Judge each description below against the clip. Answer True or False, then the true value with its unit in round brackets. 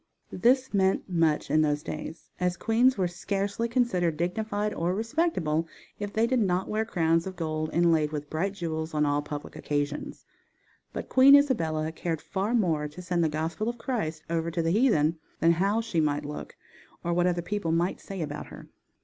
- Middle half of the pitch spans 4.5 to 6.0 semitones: True (4.9 semitones)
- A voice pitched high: False (175 Hz)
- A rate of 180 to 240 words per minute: True (185 wpm)